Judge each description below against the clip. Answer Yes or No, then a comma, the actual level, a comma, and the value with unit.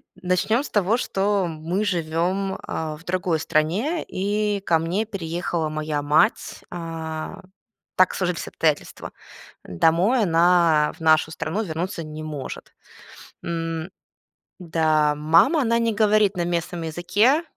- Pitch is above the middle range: No, medium, 170 Hz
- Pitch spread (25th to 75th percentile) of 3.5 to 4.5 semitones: Yes, average, 3.8 semitones